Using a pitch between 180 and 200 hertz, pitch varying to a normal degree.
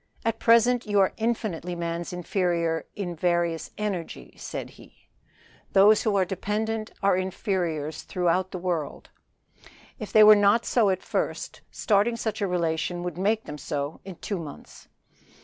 Yes: medium, 185 Hz; average, 3.8 semitones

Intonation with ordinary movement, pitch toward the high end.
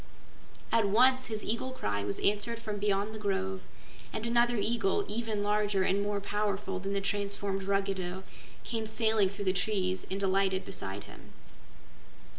No: narrow, 2.1 semitones; high, 200 Hz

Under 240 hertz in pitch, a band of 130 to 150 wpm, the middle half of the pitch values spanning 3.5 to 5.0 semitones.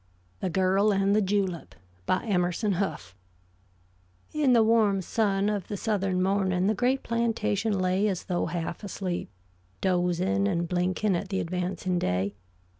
No: high, 190 Hz; average, 145 wpm; narrow, 2.5 semitones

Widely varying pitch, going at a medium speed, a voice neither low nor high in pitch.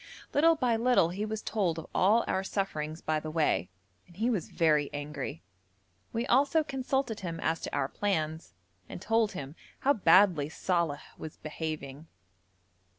Yes: wide, 6.4 semitones; average, 150 wpm; medium, 175 Hz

